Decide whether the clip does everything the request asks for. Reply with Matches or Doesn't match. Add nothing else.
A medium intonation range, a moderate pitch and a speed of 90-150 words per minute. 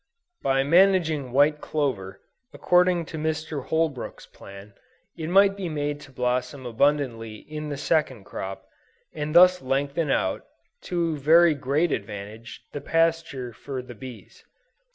Matches